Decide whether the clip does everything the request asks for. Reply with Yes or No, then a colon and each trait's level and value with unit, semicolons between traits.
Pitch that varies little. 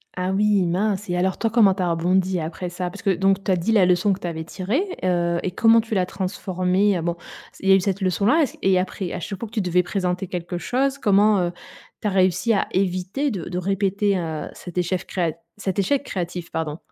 Yes: narrow, 2.3 semitones